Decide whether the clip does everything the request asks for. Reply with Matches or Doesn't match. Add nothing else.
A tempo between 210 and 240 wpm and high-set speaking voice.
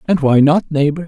Doesn't match